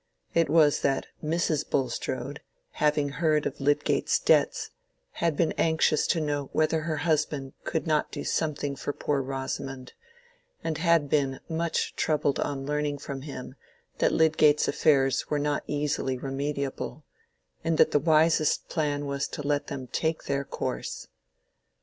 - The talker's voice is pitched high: No, medium, 145 Hz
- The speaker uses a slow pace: No, average, 145 wpm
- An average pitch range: No, narrow, 2.0 semitones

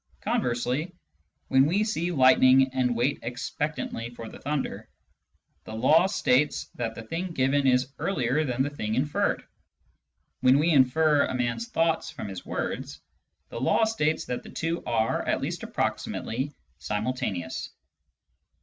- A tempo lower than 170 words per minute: Yes, average, 140 wpm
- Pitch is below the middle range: Yes, low, 130 Hz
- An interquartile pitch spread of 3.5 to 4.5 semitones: Yes, average, 4.2 semitones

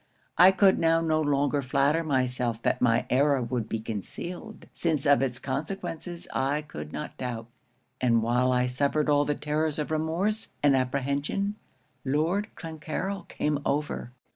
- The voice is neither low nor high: Yes, medium, 145 Hz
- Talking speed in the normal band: Yes, average, 150 wpm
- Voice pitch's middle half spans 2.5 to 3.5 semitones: No, average, 3.9 semitones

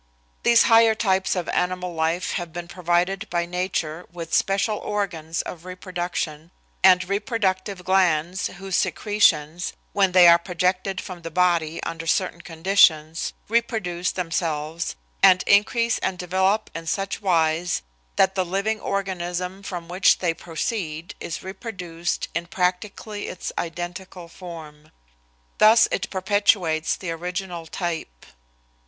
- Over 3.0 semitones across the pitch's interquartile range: No, narrow, 2.5 semitones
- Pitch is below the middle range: No, medium, 180 Hz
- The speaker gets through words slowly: Yes, slow, 125 wpm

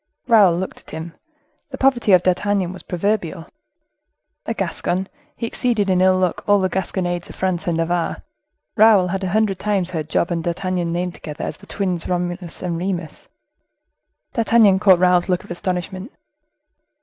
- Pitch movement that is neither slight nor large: No, narrow, 2.3 semitones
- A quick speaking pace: No, average, 165 wpm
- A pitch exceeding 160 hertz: Yes, medium, 185 Hz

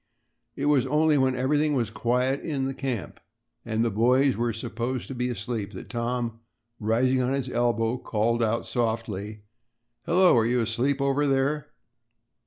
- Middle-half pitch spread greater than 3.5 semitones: No, average, 2.9 semitones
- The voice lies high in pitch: No, low, 125 Hz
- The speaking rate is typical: Yes, average, 160 wpm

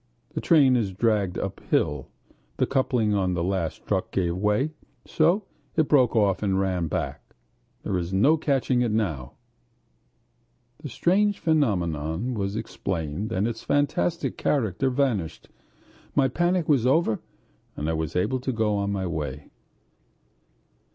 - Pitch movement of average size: No, wide, 6.7 semitones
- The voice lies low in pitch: Yes, low, 105 Hz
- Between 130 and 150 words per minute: Yes, average, 140 wpm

